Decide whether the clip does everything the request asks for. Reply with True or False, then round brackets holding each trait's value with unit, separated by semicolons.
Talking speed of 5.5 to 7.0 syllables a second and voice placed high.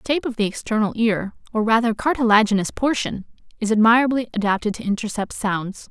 True (6.3 syllables/s; 220 Hz)